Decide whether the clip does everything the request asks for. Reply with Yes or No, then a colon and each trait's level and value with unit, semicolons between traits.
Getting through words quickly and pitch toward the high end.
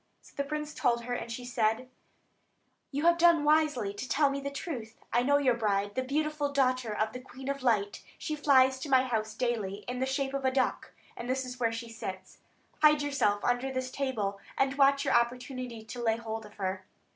Yes: fast, 215 wpm; very high, 255 Hz